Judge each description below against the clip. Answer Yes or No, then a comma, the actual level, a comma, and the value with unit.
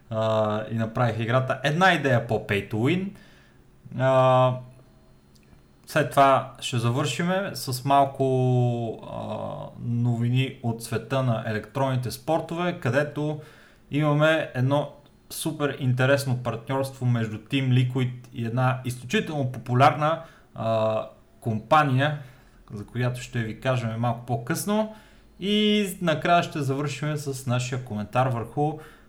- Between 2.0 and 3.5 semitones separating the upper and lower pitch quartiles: No, average, 3.9 semitones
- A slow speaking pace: Yes, slow, 110 wpm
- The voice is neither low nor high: No, low, 130 Hz